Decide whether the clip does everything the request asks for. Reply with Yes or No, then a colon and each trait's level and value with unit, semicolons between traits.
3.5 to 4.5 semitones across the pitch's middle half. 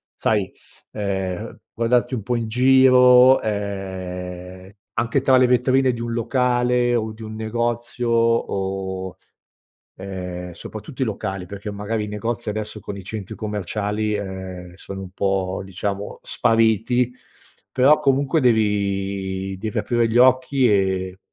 Yes: average, 4.0 semitones